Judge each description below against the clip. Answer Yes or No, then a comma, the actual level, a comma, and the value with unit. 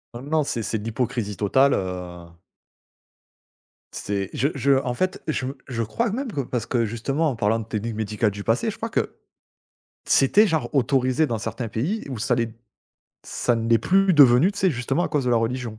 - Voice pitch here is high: No, low, 120 Hz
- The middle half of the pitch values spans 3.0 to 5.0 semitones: Yes, average, 4.2 semitones